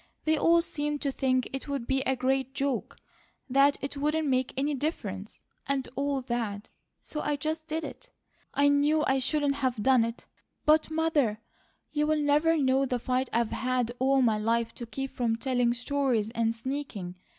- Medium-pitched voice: No, very high, 270 Hz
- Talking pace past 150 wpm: Yes, average, 175 wpm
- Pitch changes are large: No, average, 3.3 semitones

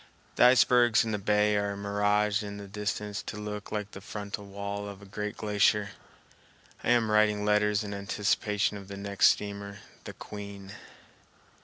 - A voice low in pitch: Yes, low, 105 Hz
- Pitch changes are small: Yes, narrow, 0.7 semitones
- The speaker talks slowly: No, average, 165 wpm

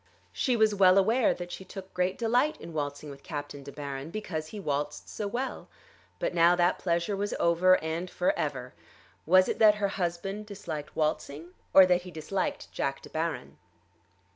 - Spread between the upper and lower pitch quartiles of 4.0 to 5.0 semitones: Yes, average, 4.3 semitones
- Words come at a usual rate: Yes, average, 180 wpm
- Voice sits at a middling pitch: Yes, medium, 175 Hz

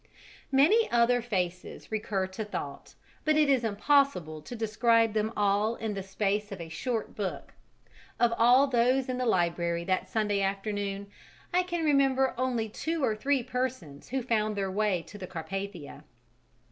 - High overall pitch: Yes, high, 215 Hz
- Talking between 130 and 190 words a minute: Yes, average, 160 wpm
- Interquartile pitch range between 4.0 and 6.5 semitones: Yes, average, 4.6 semitones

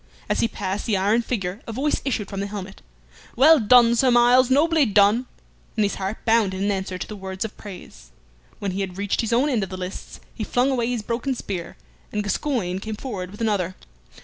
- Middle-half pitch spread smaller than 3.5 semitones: No, average, 3.9 semitones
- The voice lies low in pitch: No, high, 210 Hz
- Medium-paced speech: No, fast, 215 wpm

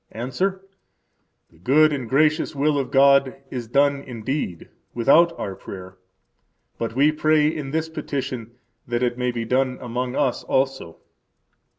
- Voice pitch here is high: No, low, 135 Hz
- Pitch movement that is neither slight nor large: Yes, average, 3.8 semitones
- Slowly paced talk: No, average, 145 wpm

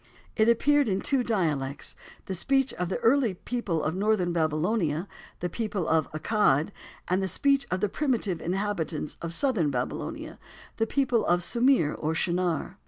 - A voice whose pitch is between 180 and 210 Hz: Yes, high, 190 Hz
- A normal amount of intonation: No, wide, 6.1 semitones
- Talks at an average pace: Yes, average, 145 wpm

